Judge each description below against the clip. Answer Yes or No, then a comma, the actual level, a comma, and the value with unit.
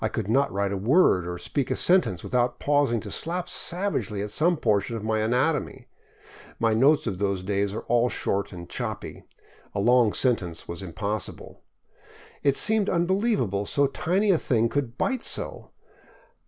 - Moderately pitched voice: No, low, 115 Hz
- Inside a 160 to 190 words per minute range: Yes, average, 170 wpm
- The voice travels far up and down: Yes, wide, 6.9 semitones